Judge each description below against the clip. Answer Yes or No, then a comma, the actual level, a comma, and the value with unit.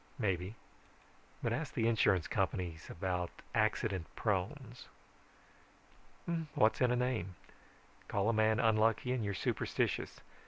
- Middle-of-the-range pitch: No, low, 110 Hz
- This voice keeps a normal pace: No, slow, 115 wpm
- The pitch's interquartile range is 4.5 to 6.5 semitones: No, average, 4.0 semitones